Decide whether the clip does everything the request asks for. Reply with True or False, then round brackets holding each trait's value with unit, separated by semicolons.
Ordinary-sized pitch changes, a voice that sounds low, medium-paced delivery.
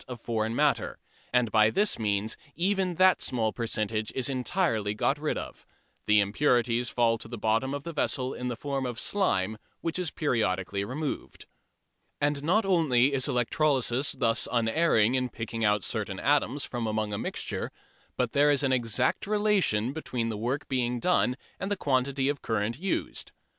True (4.7 semitones; 125 Hz; 170 wpm)